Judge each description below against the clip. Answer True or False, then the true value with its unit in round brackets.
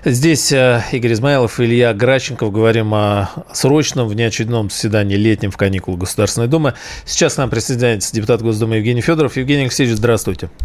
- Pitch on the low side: True (115 Hz)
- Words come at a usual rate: True (150 wpm)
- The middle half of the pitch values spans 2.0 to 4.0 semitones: True (3.4 semitones)